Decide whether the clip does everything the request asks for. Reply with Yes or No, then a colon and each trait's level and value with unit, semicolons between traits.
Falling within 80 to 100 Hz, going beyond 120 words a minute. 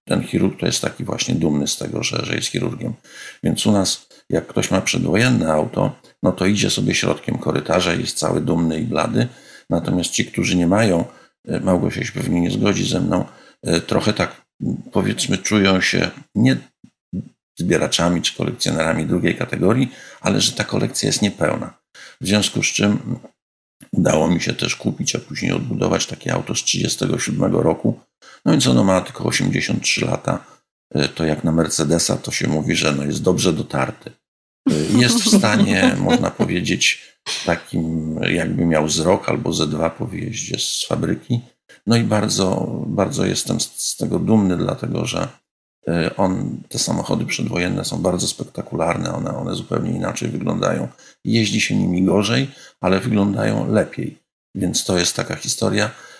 Yes: very low, 90 Hz; fast, 160 wpm